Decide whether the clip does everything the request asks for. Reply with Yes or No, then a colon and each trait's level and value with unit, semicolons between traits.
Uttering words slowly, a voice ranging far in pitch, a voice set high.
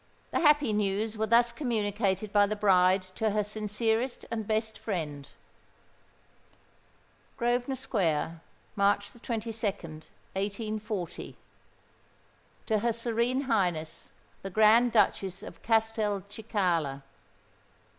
No: slow, 95 wpm; average, 2.8 semitones; high, 215 Hz